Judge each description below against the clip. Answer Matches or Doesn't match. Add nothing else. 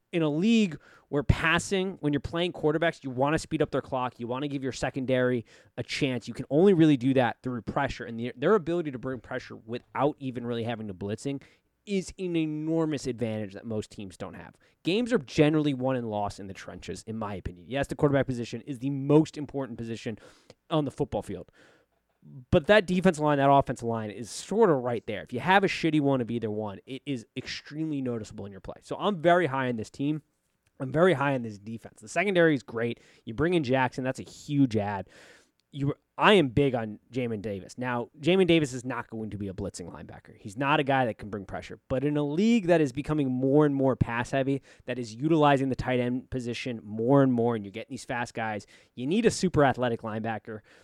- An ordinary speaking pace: Doesn't match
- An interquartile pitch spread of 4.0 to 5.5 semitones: Matches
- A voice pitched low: Matches